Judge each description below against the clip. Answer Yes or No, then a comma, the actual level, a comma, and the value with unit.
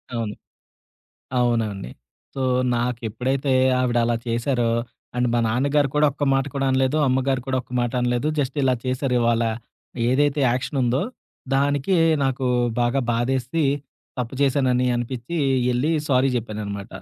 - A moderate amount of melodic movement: No, narrow, 2.3 semitones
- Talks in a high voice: No, low, 125 Hz